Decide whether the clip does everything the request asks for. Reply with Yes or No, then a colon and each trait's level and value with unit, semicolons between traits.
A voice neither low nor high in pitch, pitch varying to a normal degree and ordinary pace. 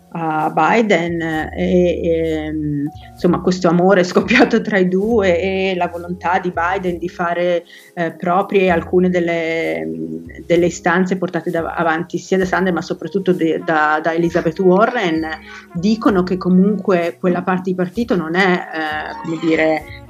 No: medium, 175 Hz; narrow, 2.2 semitones; average, 145 wpm